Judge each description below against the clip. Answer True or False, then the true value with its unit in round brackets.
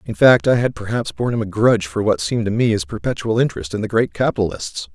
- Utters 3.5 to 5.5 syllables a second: False (6.7 syllables/s)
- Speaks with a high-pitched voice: False (105 Hz)